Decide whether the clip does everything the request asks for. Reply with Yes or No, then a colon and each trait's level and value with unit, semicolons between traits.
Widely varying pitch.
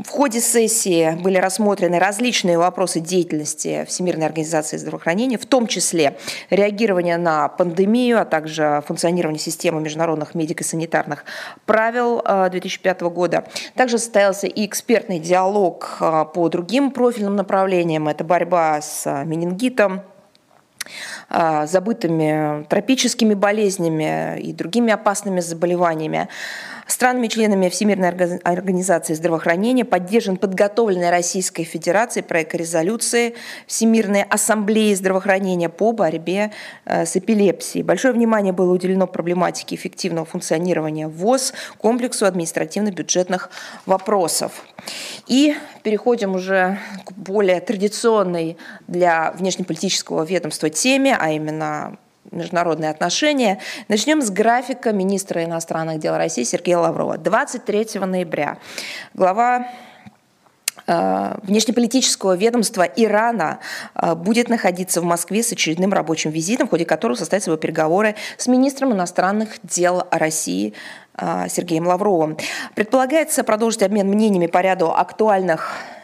No: average, 4.5 semitones